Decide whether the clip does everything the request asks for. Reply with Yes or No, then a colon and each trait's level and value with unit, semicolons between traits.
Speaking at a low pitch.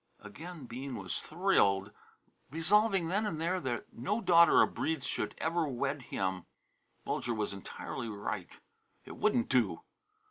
No: medium, 145 Hz